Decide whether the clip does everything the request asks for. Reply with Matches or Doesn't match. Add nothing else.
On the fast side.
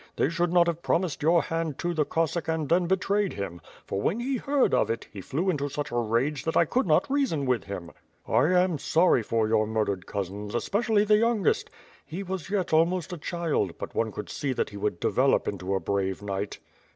Matches